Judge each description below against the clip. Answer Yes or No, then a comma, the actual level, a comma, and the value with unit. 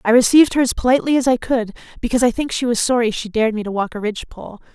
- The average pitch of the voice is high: Yes, high, 235 Hz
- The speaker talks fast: Yes, fast, 265 wpm